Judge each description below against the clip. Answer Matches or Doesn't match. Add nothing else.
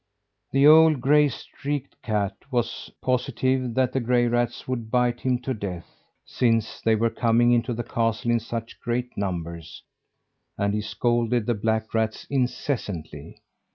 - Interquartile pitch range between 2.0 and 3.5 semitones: Matches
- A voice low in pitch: Matches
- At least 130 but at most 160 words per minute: Matches